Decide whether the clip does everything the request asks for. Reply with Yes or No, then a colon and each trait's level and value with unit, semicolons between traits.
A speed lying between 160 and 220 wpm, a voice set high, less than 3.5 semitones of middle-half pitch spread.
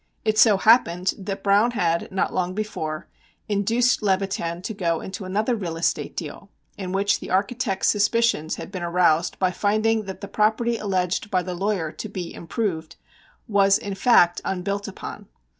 Yes: average, 165 wpm; high, 195 Hz; average, 2.9 semitones